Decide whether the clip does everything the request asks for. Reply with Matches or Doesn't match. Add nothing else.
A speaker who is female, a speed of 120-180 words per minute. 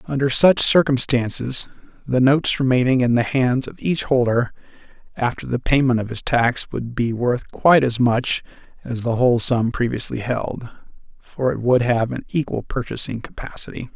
Doesn't match